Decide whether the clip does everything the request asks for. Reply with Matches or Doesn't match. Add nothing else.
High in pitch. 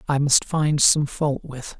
Doesn't match